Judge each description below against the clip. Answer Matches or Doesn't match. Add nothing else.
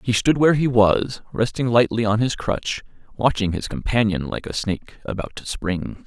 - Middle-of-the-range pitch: Doesn't match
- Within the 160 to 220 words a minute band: Matches